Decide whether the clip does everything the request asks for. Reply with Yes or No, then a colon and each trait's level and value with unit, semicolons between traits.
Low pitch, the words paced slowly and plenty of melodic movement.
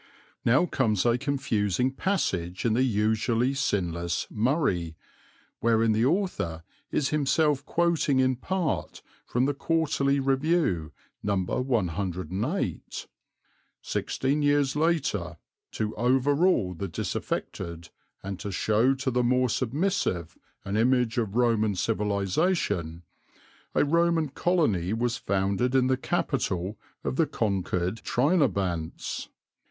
Yes: low, 120 Hz; slow, 110 wpm; wide, 6.3 semitones